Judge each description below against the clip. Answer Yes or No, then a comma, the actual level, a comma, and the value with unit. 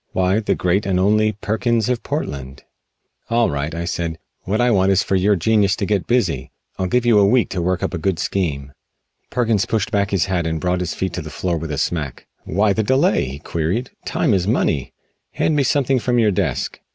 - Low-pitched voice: Yes, very low, 95 Hz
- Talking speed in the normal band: No, fast, 220 wpm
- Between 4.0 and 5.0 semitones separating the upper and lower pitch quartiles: Yes, average, 4.6 semitones